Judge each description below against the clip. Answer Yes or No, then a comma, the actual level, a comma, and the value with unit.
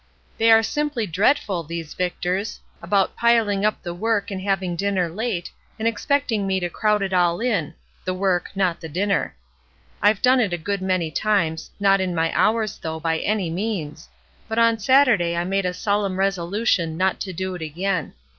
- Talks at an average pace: Yes, average, 185 wpm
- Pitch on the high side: Yes, high, 195 Hz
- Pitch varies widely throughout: No, average, 3.6 semitones